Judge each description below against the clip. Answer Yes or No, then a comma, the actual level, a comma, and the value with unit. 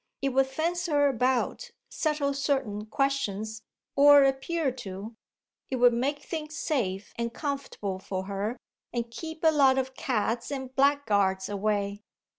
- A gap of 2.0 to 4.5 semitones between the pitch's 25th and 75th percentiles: No, average, 5.0 semitones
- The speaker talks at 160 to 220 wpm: No, average, 140 wpm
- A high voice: Yes, very high, 260 Hz